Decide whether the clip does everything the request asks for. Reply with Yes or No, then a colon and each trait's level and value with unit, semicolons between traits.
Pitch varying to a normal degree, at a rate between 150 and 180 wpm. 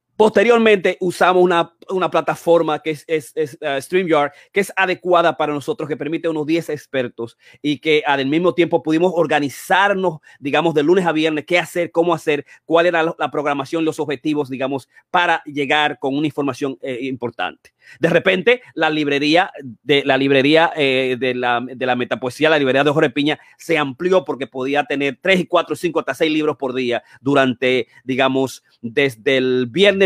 Yes: average, 3.6 semitones; average, 170 wpm